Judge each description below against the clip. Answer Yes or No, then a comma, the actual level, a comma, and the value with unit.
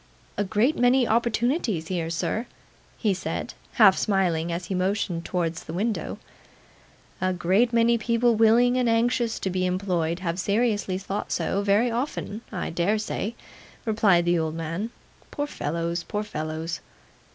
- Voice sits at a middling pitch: No, high, 200 Hz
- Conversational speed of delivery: Yes, average, 150 wpm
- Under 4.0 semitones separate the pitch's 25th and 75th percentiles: No, average, 4.9 semitones